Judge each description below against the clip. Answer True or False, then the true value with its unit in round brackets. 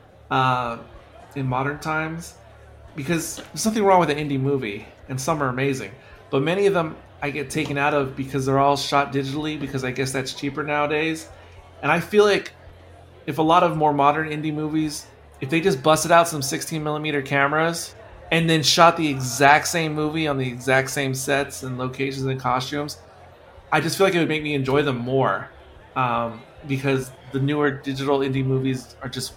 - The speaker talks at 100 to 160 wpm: False (190 wpm)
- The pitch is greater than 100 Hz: True (140 Hz)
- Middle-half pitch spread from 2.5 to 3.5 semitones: True (3.0 semitones)